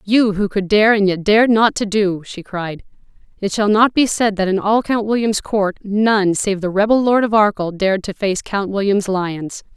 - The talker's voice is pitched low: No, high, 205 Hz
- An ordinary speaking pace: No, fast, 220 wpm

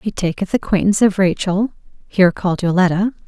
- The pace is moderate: Yes, average, 145 wpm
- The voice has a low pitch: No, high, 190 Hz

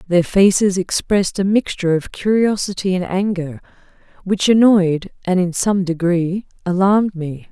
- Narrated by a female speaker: Yes, female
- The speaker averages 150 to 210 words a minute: No, slow, 135 wpm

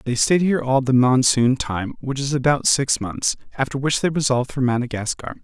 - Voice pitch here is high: No, low, 130 Hz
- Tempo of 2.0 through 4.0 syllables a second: No, 5.5 syllables/s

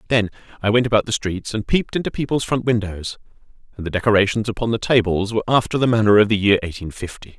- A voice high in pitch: No, low, 110 Hz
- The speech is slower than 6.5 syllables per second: No, 6.8 syllables/s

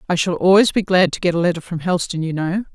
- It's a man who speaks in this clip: No, female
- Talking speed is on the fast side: Yes, fast, 285 wpm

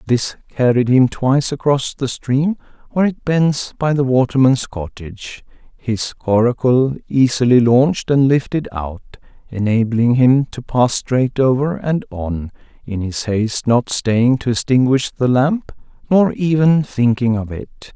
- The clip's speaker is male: Yes, male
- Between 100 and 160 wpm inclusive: Yes, average, 145 wpm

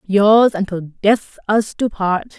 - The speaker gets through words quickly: No, average, 150 wpm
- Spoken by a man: No, female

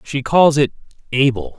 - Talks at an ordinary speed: Yes, average, 150 wpm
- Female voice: No, male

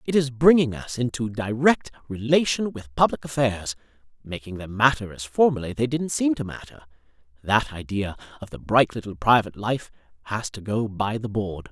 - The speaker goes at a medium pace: Yes, average, 170 wpm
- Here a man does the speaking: Yes, male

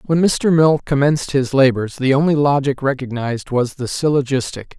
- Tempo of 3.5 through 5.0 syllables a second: No, 5.2 syllables/s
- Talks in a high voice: No, low, 135 Hz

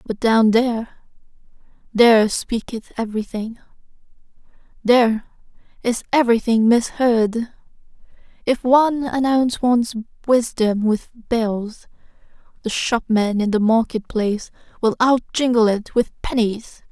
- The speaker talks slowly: Yes, slow, 100 wpm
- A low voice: No, high, 230 Hz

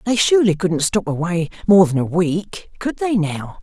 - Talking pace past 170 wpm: Yes, average, 200 wpm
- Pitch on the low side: No, medium, 185 Hz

